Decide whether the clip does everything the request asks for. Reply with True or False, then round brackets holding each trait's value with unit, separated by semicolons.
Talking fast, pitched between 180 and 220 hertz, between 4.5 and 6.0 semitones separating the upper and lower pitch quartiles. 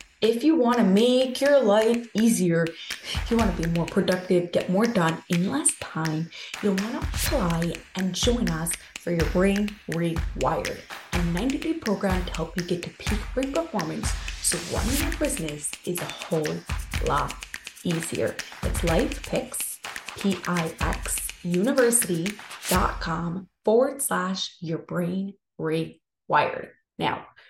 False (140 wpm; 190 Hz; 5.4 semitones)